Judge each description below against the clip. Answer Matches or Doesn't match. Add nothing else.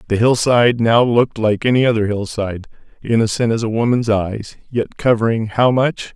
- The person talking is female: Doesn't match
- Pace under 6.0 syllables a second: Matches